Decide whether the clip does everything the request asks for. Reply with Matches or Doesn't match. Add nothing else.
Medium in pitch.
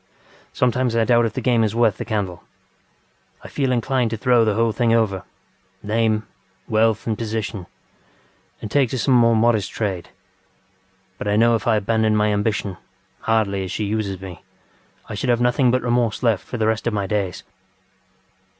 Doesn't match